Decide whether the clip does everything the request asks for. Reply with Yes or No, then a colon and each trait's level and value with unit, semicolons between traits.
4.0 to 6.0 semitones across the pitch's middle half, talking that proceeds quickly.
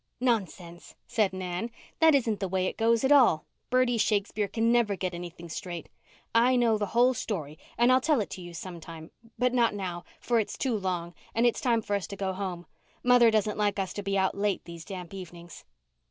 Yes: average, 4.7 semitones; fast, 210 wpm